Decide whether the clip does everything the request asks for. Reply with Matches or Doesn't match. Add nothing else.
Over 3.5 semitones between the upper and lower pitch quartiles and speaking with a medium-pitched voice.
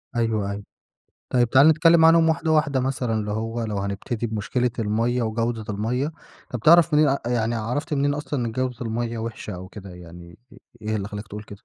Doesn't match